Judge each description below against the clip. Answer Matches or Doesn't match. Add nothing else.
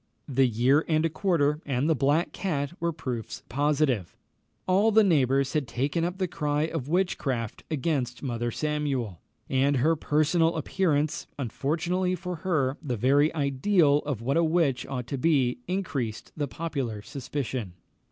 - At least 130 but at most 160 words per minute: Matches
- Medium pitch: Matches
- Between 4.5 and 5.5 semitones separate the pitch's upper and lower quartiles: Doesn't match